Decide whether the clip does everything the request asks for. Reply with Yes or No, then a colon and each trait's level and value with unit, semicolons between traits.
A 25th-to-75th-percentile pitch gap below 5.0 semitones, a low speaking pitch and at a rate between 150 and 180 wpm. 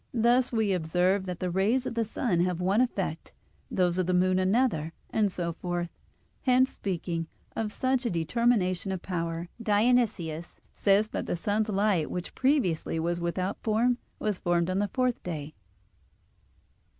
No: average, 4.4 semitones; high, 190 Hz; average, 170 wpm